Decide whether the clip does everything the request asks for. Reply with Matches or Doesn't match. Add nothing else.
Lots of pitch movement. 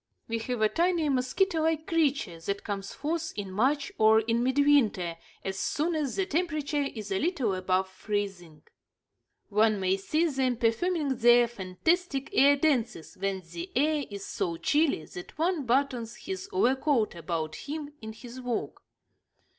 Matches